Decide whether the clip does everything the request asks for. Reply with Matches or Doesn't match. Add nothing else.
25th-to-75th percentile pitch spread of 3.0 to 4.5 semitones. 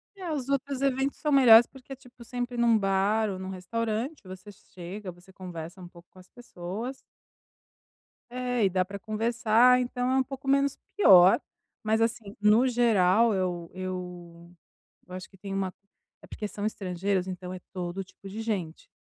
Doesn't match